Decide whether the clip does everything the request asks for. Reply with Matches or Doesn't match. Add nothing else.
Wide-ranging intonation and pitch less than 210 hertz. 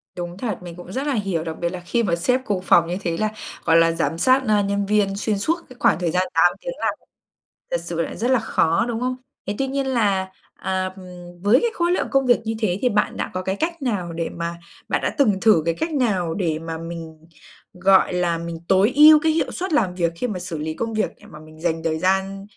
Matches